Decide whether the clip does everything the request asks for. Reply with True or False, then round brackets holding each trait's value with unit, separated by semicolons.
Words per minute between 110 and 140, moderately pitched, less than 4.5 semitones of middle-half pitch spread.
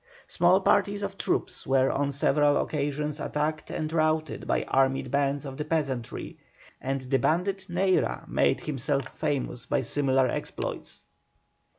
True (135 wpm; 145 Hz; 2.8 semitones)